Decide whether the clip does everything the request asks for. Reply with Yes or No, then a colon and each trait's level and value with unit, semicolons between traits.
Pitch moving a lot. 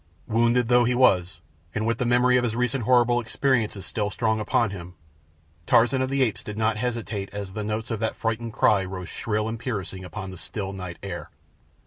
No: average, 3.4 semitones